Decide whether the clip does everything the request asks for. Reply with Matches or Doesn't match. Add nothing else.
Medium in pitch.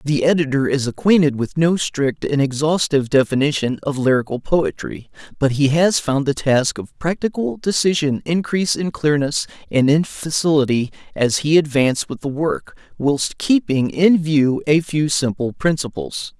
Matches